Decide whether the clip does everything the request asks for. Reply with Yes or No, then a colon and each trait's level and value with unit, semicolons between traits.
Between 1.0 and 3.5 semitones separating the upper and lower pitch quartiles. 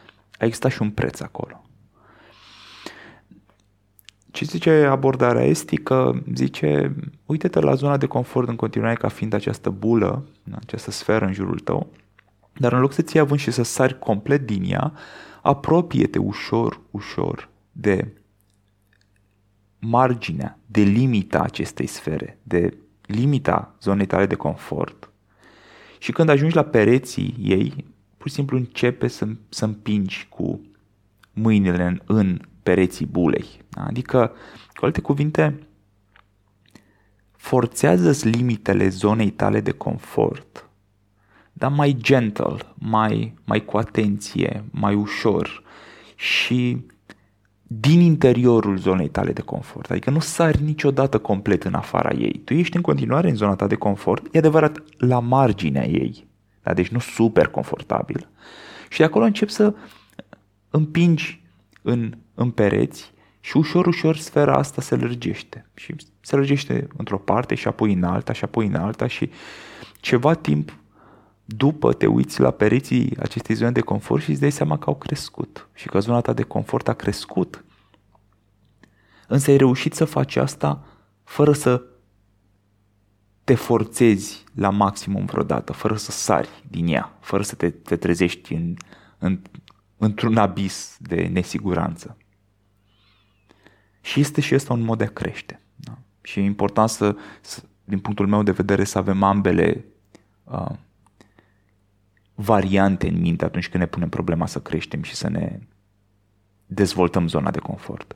No: average, 4.4 semitones